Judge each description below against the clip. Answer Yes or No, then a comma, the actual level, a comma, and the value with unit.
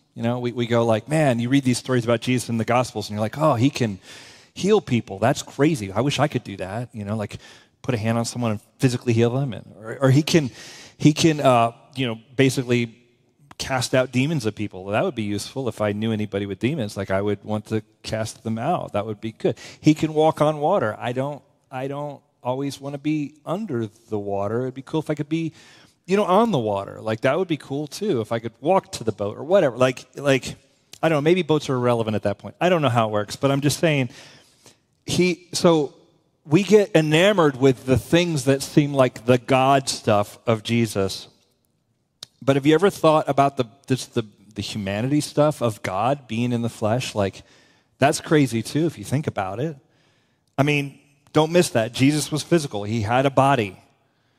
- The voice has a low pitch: Yes, low, 130 Hz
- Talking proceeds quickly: Yes, fast, 225 wpm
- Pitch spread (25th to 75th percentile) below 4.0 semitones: No, average, 4.6 semitones